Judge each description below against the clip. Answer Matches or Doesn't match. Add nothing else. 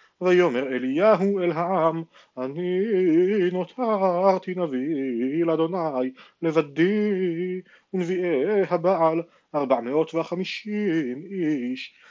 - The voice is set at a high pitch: Doesn't match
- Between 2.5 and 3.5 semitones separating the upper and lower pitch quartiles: Matches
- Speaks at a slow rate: Matches